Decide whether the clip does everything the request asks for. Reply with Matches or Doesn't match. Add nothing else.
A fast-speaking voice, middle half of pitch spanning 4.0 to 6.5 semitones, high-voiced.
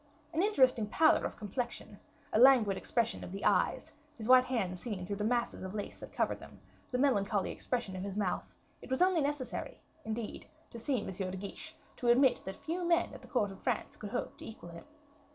Matches